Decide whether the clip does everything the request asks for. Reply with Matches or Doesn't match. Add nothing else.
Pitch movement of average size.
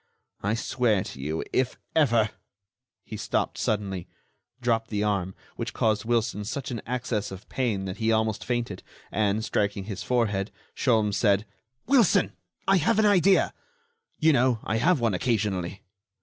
Matches